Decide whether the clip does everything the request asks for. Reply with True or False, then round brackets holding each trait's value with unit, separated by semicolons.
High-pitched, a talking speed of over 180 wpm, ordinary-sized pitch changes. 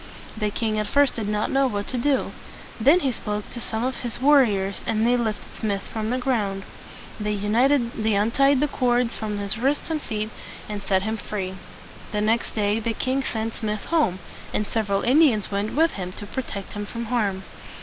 True (220 Hz; 195 wpm; 3.4 semitones)